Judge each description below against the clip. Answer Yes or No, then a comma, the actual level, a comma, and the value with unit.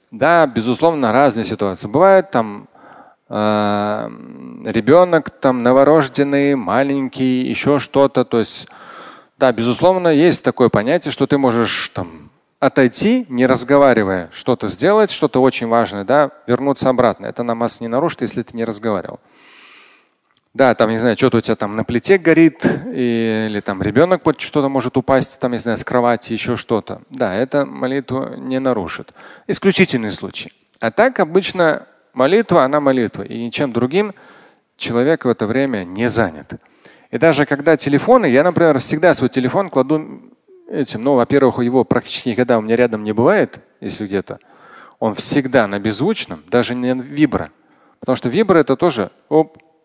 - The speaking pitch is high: No, low, 130 Hz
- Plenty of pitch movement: No, average, 4.5 semitones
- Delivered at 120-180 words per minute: Yes, average, 150 wpm